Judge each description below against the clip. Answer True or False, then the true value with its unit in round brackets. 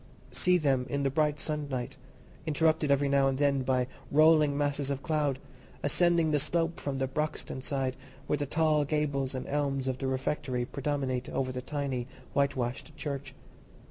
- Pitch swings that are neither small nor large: False (2.3 semitones)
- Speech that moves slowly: False (165 wpm)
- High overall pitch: False (140 Hz)